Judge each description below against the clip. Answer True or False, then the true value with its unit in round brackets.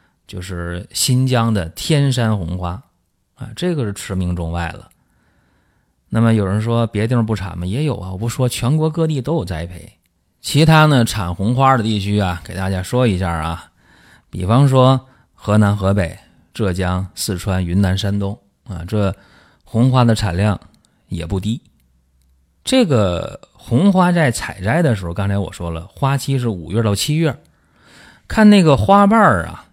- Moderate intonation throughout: False (6.0 semitones)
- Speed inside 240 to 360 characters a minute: False (230 characters per minute)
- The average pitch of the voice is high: False (105 Hz)